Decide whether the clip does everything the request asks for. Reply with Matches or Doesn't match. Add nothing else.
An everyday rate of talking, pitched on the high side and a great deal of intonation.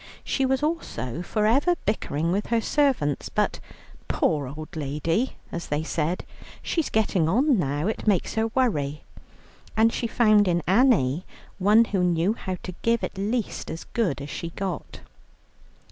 Matches